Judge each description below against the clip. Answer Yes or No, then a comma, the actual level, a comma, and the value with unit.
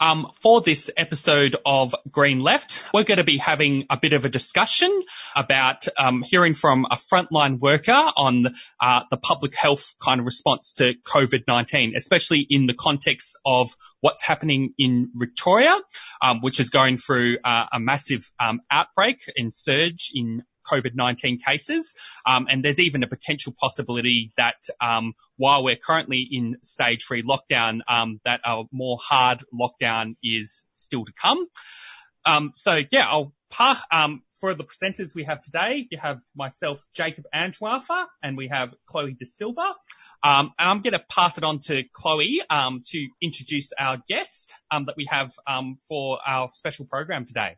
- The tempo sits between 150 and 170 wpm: Yes, average, 165 wpm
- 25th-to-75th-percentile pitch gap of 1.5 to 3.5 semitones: No, average, 4.1 semitones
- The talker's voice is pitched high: No, medium, 140 Hz